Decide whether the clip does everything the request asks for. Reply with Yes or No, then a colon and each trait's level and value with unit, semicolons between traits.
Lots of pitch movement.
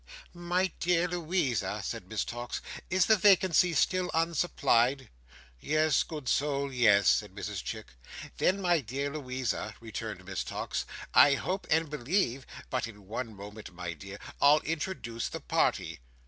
Yes: wide, 7.4 semitones